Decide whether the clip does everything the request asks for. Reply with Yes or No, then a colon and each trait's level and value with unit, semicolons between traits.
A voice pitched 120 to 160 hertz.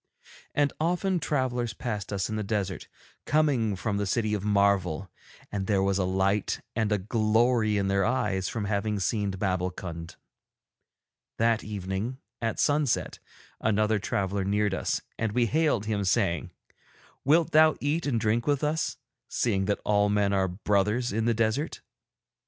No: low, 105 Hz